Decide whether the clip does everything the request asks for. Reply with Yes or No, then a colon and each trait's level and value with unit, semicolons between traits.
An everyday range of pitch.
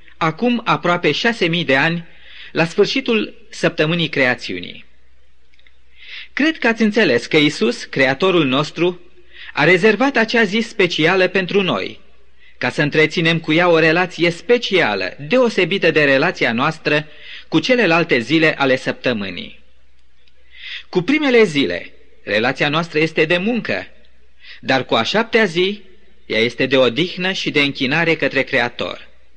No: wide, 6.6 semitones